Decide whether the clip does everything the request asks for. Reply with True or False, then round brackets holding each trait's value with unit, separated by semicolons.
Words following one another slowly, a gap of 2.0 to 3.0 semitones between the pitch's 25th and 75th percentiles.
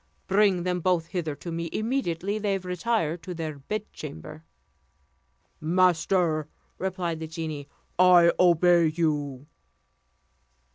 True (105 wpm; 2.6 semitones)